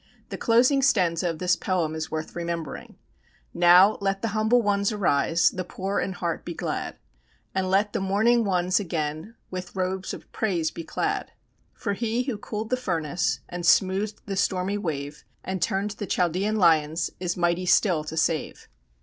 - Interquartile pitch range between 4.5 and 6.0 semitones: No, average, 3.3 semitones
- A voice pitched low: No, medium, 185 Hz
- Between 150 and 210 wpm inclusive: Yes, average, 170 wpm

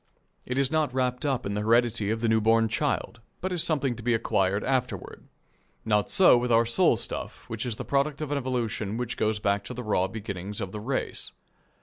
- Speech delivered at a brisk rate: Yes, fast, 220 wpm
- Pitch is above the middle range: No, low, 115 Hz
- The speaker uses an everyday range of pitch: Yes, average, 3.5 semitones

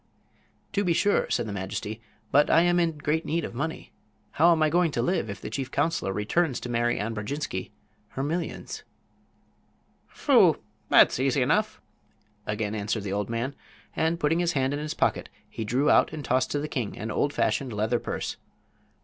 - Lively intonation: Yes, wide, 6.2 semitones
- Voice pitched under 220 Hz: Yes, medium, 140 Hz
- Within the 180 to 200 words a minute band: Yes, average, 185 wpm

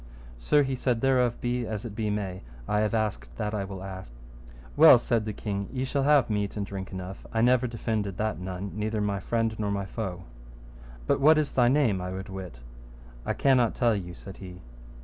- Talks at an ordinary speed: No, fast, 210 wpm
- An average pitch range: Yes, average, 3.9 semitones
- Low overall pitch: Yes, low, 105 Hz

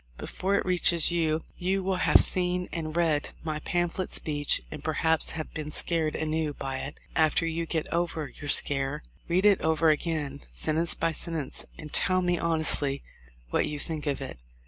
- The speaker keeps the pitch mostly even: Yes, narrow, 2.3 semitones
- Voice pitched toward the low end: No, medium, 160 Hz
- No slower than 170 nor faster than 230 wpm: Yes, average, 180 wpm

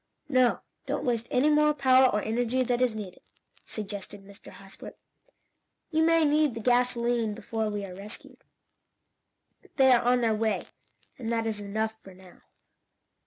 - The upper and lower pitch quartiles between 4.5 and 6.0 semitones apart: No, average, 3.3 semitones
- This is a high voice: Yes, high, 230 Hz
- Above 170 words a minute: No, average, 155 wpm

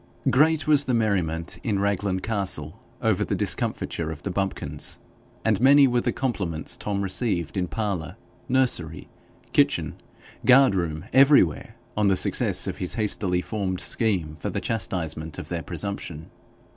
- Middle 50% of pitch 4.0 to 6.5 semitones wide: Yes, average, 5.2 semitones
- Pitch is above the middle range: No, low, 100 Hz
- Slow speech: No, average, 145 wpm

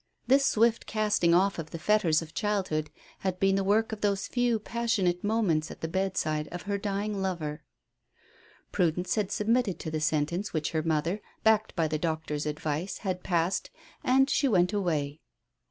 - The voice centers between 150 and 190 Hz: Yes, medium, 185 Hz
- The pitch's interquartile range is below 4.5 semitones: No, average, 4.8 semitones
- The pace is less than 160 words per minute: No, average, 170 wpm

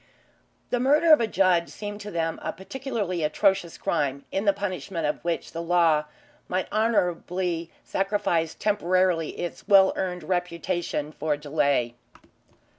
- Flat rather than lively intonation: No, average, 3.4 semitones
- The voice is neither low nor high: Yes, medium, 180 Hz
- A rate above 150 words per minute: No, slow, 135 wpm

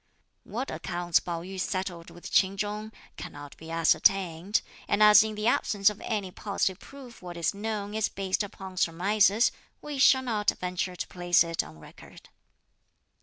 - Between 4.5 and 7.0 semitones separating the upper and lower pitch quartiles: No, average, 3.2 semitones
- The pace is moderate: Yes, average, 165 wpm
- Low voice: No, high, 195 Hz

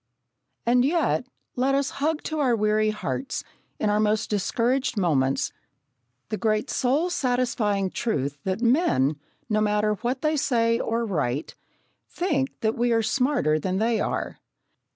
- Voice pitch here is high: Yes, high, 230 Hz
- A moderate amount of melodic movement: Yes, average, 3.9 semitones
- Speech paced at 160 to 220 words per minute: No, average, 145 wpm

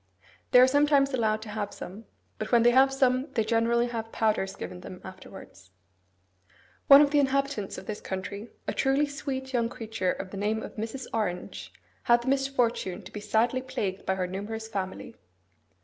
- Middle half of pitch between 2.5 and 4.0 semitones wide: No, average, 4.5 semitones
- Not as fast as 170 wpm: No, average, 180 wpm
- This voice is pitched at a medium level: No, high, 225 Hz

